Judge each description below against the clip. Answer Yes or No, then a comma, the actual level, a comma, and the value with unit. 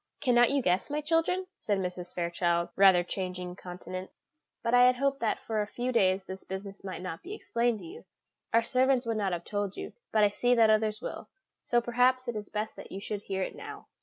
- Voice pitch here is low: No, high, 215 Hz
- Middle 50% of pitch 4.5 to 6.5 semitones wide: Yes, average, 4.8 semitones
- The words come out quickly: Yes, fast, 220 wpm